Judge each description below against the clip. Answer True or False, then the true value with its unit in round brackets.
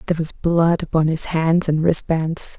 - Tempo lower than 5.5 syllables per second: True (4.6 syllables/s)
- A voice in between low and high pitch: True (165 Hz)